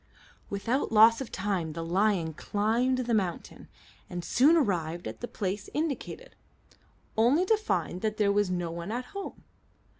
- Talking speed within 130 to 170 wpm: Yes, average, 155 wpm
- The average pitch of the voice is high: Yes, high, 210 Hz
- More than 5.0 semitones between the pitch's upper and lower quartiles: Yes, wide, 5.6 semitones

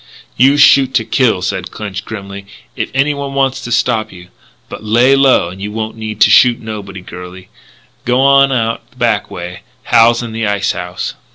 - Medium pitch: No, low, 110 Hz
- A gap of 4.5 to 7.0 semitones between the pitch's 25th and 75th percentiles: Yes, average, 4.8 semitones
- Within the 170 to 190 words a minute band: Yes, average, 180 wpm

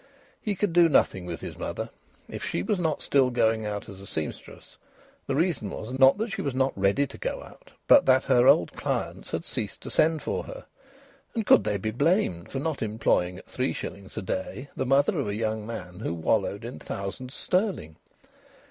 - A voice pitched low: Yes, low, 125 Hz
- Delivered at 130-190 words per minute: No, fast, 205 wpm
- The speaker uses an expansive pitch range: Yes, wide, 8.0 semitones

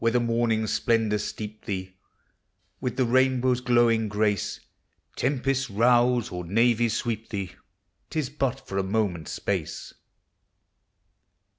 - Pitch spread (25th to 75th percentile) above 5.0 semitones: No, average, 2.9 semitones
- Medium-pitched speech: No, low, 115 Hz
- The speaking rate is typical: No, slow, 120 wpm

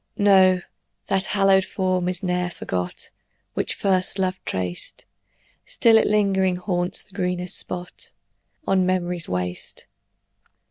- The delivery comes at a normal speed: No, slow, 120 wpm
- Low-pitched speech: No, medium, 185 Hz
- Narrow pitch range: Yes, narrow, 1.4 semitones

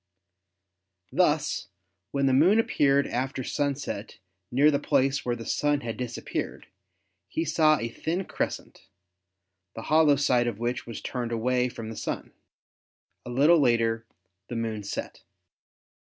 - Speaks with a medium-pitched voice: No, low, 130 Hz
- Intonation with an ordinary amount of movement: Yes, average, 3.8 semitones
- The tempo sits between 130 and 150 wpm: Yes, average, 140 wpm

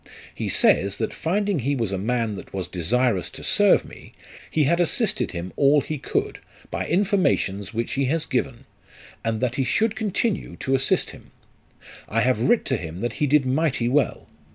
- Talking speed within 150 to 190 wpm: Yes, average, 185 wpm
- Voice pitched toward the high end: No, low, 130 Hz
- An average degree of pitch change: No, wide, 6.2 semitones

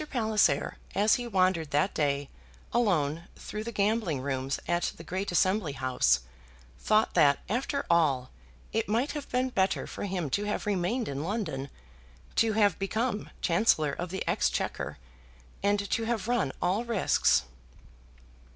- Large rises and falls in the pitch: Yes, wide, 5.9 semitones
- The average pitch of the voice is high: Yes, high, 195 Hz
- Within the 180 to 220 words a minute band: No, average, 145 wpm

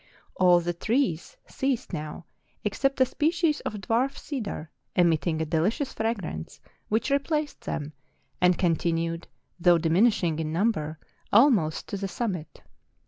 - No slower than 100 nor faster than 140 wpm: Yes, slow, 135 wpm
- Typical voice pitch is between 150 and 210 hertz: Yes, medium, 185 Hz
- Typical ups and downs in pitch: No, wide, 6.7 semitones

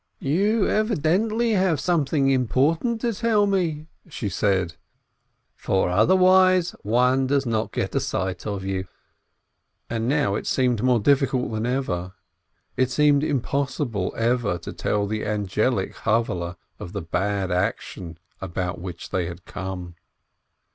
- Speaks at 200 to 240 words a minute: No, slow, 135 wpm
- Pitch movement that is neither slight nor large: No, wide, 8.0 semitones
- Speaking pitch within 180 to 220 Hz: No, low, 125 Hz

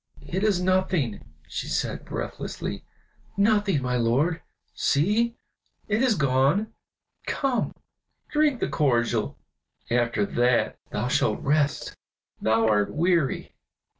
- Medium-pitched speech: Yes, medium, 150 Hz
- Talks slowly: Yes, slow, 105 wpm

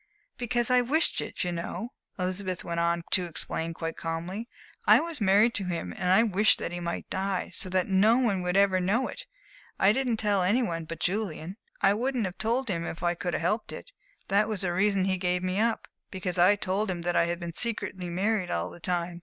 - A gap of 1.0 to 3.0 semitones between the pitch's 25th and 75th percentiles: No, average, 3.6 semitones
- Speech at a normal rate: No, fast, 225 wpm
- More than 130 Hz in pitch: Yes, medium, 185 Hz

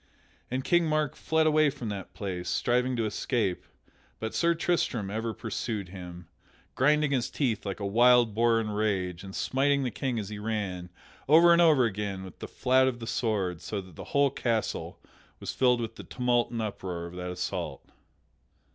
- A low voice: Yes, low, 115 Hz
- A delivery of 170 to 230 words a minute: Yes, average, 185 wpm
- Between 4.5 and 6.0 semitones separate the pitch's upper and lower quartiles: Yes, average, 4.9 semitones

